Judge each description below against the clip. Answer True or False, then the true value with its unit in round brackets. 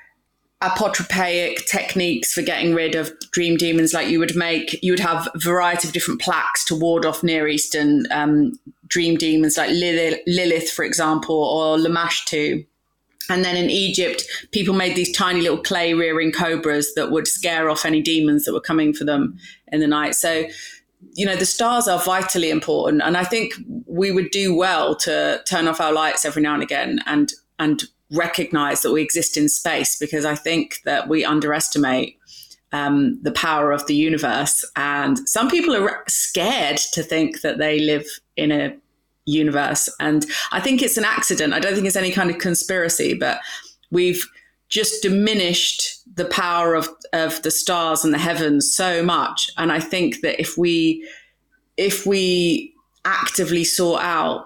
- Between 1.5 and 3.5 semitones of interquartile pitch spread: True (3.1 semitones)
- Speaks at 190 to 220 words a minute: False (175 wpm)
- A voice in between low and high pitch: True (165 Hz)